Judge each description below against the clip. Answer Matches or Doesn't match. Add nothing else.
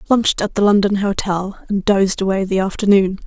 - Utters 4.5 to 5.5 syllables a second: Doesn't match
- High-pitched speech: Matches